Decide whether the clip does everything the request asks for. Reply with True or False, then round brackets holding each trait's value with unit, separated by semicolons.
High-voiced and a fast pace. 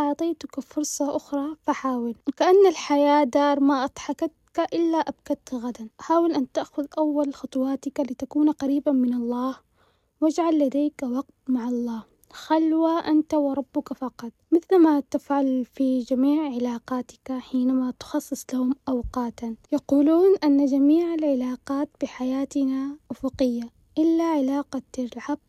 False (280 Hz; 115 wpm)